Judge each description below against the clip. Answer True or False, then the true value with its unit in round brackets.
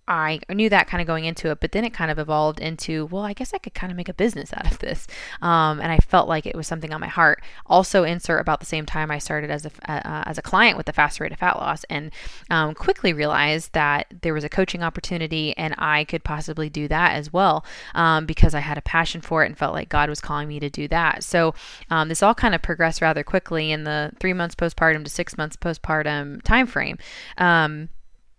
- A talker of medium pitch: True (160 Hz)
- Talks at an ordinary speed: False (245 wpm)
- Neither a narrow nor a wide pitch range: False (2.3 semitones)